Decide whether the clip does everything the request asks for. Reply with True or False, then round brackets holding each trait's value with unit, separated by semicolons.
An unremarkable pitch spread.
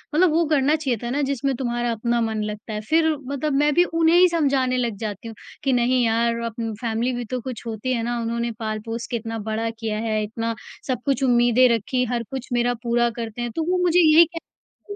True (3.3 semitones)